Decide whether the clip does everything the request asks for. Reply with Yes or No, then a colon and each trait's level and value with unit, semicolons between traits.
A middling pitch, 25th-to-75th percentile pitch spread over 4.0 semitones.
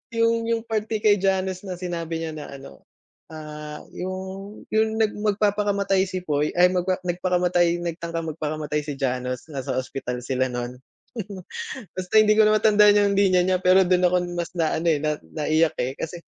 Yes: medium, 180 Hz; average, 4.5 semitones